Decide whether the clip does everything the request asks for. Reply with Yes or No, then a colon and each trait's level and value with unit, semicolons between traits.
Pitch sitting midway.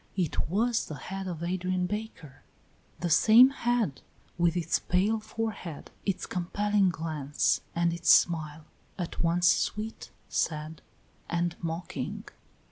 Yes: medium, 175 Hz